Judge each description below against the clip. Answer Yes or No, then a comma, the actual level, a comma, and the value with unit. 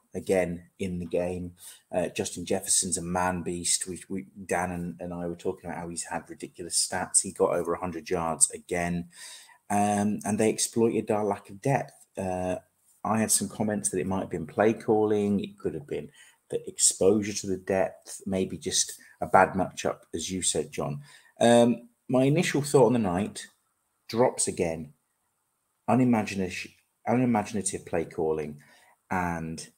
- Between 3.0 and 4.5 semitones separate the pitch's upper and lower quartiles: Yes, average, 3.5 semitones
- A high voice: No, very low, 95 Hz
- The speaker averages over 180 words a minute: No, average, 165 wpm